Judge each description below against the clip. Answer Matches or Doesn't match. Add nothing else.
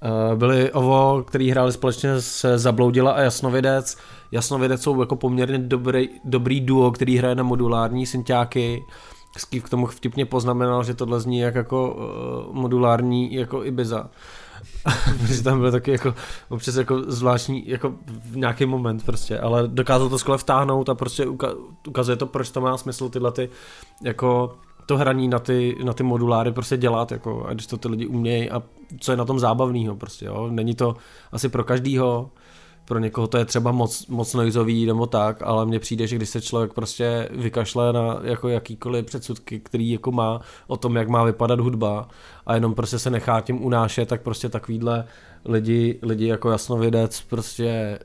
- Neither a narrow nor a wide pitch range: Doesn't match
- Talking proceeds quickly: Matches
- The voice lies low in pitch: Matches